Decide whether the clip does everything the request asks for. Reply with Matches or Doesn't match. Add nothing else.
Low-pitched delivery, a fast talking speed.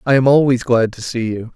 Matches